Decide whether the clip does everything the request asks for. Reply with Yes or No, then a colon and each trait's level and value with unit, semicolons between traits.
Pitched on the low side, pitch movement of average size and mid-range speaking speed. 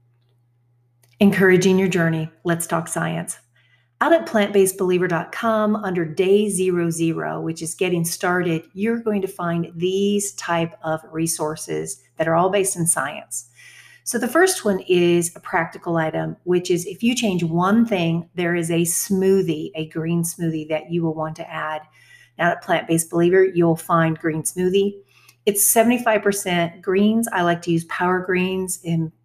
No: medium, 170 Hz; average, 3.0 semitones; average, 160 wpm